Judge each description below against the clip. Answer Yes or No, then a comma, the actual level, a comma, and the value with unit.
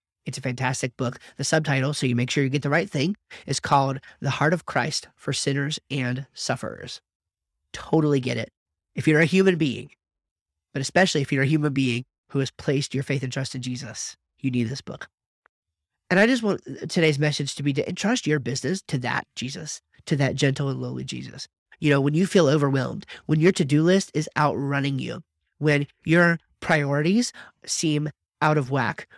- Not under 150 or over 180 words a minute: No, average, 195 wpm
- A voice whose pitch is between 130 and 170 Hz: Yes, medium, 140 Hz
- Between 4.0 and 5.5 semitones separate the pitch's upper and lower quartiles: No, average, 3.3 semitones